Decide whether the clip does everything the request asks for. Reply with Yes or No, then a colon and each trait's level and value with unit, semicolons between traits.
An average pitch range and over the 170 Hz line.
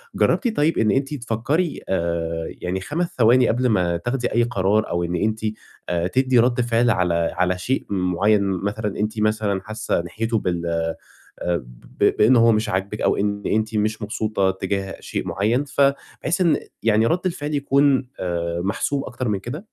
No: average, 4.8 semitones; low, 110 Hz